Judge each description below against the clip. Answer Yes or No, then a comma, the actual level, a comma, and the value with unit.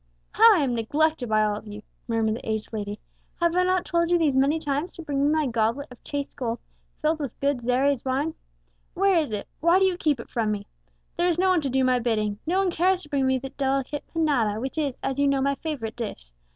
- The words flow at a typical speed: No, fast, 245 wpm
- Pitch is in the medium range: No, very high, 275 Hz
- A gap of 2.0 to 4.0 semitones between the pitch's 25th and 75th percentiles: No, wide, 5.5 semitones